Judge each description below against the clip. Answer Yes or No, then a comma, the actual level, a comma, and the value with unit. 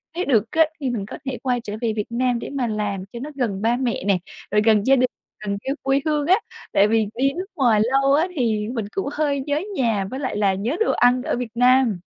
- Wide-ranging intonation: No, average, 4.2 semitones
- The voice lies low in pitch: No, high, 245 Hz